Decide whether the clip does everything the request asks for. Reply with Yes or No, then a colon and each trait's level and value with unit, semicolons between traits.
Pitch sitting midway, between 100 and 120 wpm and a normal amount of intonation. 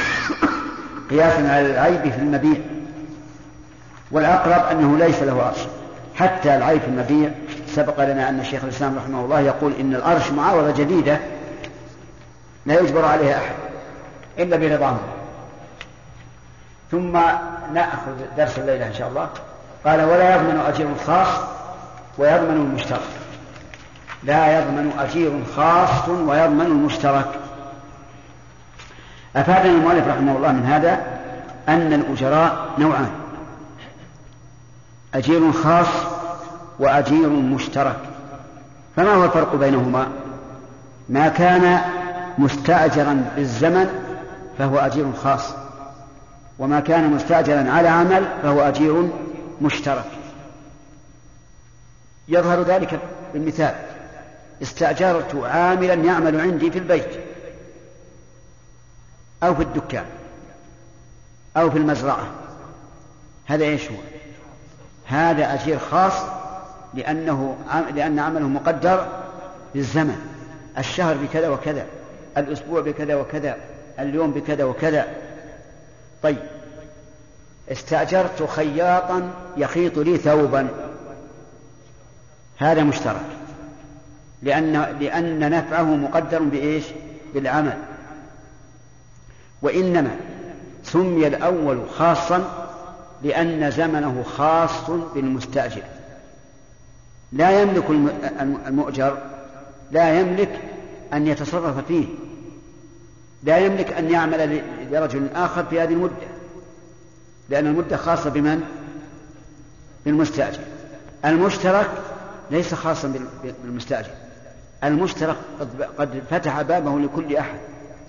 No: medium, 150 Hz; average, 90 wpm; average, 3.1 semitones